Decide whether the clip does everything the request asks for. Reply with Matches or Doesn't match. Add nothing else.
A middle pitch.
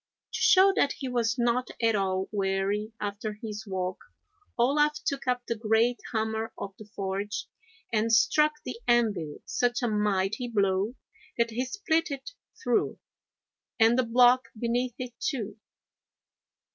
Doesn't match